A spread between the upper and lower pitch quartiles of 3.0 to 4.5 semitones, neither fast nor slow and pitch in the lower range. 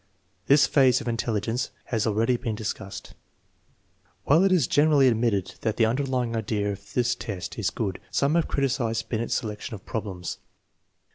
Yes: average, 3.5 semitones; average, 165 wpm; low, 115 Hz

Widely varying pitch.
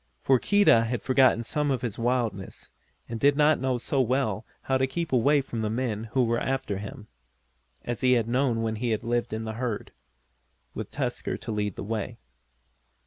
No: average, 3.0 semitones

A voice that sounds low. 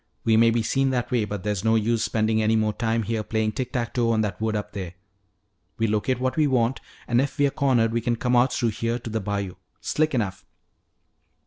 Yes: low, 115 Hz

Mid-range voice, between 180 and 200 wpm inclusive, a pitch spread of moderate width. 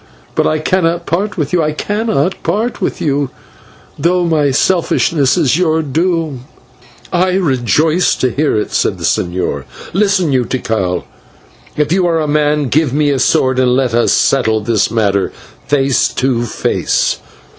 No: medium, 150 Hz; average, 155 wpm; average, 5.0 semitones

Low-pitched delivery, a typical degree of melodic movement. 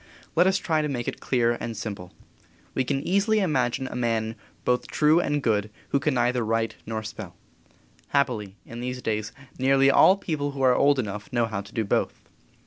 Yes: low, 125 Hz; average, 4.3 semitones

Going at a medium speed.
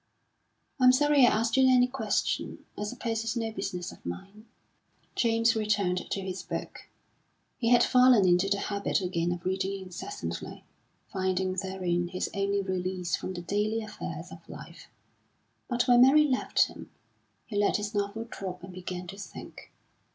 Yes: average, 160 wpm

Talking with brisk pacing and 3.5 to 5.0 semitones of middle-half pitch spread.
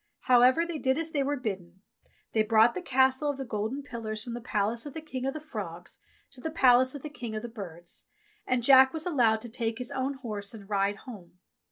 Yes: fast, 230 wpm; average, 3.8 semitones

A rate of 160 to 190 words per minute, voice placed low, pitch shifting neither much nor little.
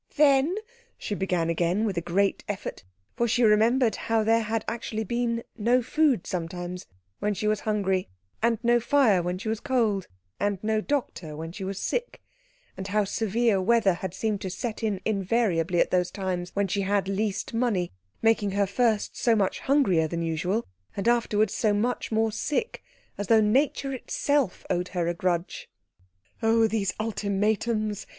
No: average, 170 wpm; high, 210 Hz; average, 3.5 semitones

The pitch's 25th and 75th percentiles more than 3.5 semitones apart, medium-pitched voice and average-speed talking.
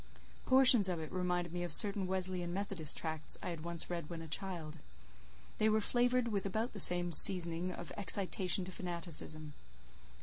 No: average, 2.7 semitones; medium, 180 Hz; average, 170 wpm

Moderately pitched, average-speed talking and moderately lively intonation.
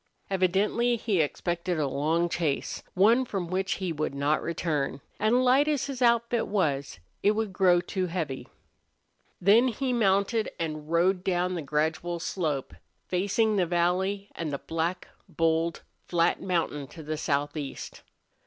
Yes: medium, 180 Hz; average, 145 wpm; average, 4.2 semitones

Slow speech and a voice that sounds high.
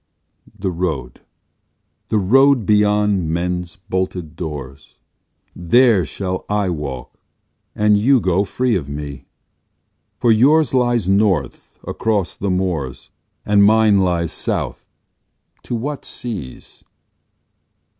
No: slow, 105 wpm; very low, 95 Hz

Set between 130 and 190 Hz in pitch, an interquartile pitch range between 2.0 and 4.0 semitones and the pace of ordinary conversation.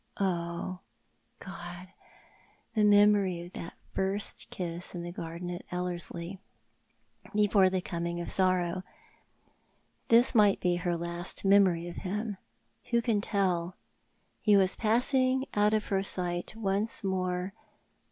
No: medium, 185 Hz; average, 2.8 semitones; slow, 125 wpm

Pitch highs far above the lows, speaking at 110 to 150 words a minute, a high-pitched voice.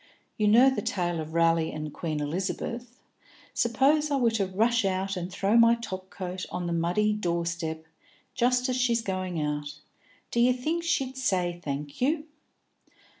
No: wide, 6.2 semitones; average, 165 wpm; high, 195 Hz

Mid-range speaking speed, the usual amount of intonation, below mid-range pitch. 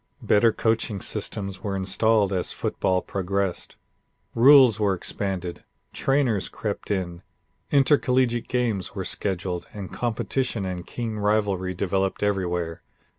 No: slow, 115 wpm; average, 3.4 semitones; low, 100 Hz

